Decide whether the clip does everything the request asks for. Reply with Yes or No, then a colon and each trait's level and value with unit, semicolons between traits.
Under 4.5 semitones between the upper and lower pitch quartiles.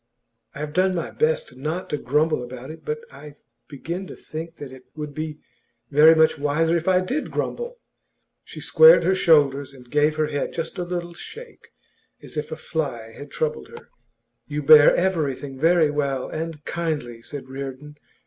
Yes: average, 3.2 semitones